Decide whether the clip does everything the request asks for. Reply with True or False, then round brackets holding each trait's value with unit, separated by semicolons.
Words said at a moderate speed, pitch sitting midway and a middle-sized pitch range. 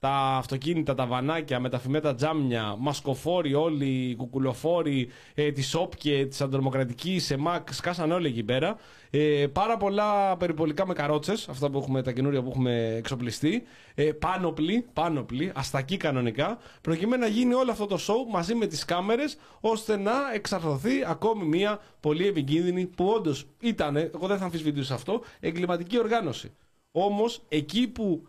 False (150 wpm; 155 Hz; 5.9 semitones)